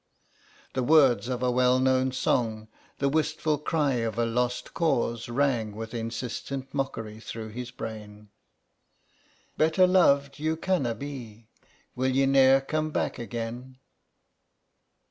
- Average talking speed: No, slow, 130 wpm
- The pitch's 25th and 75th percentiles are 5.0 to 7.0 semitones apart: No, average, 3.5 semitones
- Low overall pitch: Yes, low, 125 Hz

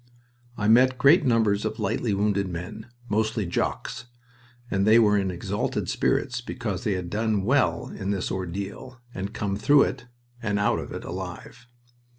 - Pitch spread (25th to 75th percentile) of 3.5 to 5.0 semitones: No, average, 3.0 semitones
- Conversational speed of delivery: Yes, average, 170 wpm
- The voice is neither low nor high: No, low, 105 Hz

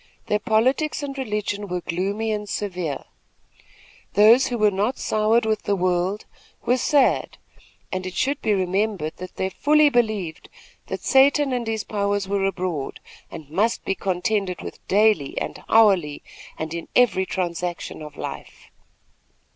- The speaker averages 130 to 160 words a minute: Yes, average, 145 wpm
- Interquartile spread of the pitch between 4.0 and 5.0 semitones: No, average, 3.5 semitones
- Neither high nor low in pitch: No, high, 205 Hz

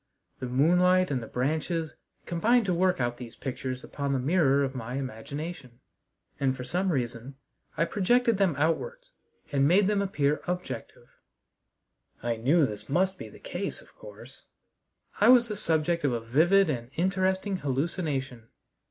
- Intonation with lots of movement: Yes, wide, 6.1 semitones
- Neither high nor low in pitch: Yes, medium, 155 Hz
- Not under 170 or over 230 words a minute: No, average, 155 wpm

